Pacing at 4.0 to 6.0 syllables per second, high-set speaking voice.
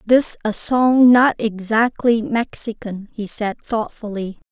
No: 3.6 syllables/s; high, 225 Hz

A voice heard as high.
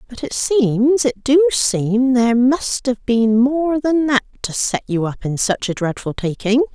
Yes: very high, 250 Hz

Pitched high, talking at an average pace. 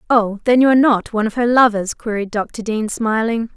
No: high, 225 Hz; fast, 220 wpm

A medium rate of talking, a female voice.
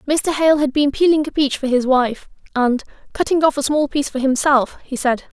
No: fast, 225 wpm; female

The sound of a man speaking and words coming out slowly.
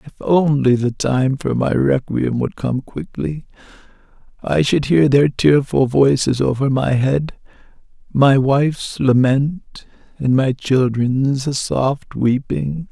Yes: male; slow, 125 wpm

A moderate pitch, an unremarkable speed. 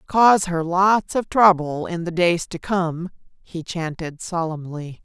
Yes: medium, 175 Hz; average, 155 wpm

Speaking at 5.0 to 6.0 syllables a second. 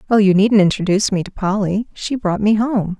Yes: 5.5 syllables/s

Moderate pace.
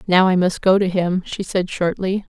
No: fast, 230 wpm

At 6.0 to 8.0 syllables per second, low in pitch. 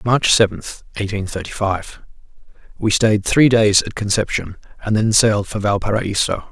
No: 4.8 syllables/s; low, 105 Hz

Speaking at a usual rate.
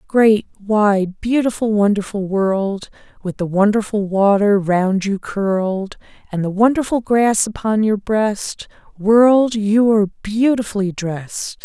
No: slow, 125 wpm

